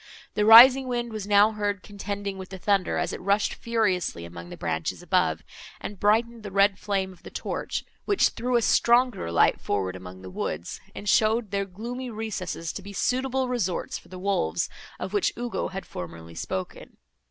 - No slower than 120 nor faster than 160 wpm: No, average, 185 wpm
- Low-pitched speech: No, high, 200 Hz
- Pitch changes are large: No, average, 3.9 semitones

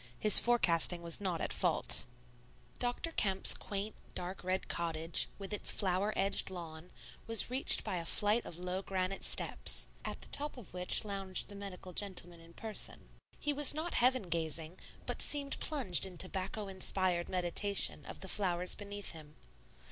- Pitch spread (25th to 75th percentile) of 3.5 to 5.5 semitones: No, average, 3.0 semitones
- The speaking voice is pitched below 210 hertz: Yes, high, 190 Hz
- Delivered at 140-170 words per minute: Yes, average, 165 wpm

